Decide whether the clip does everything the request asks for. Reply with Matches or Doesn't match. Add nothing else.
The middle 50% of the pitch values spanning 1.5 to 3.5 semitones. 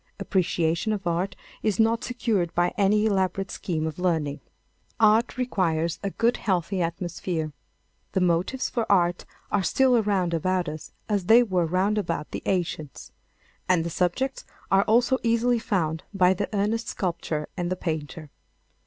Doesn't match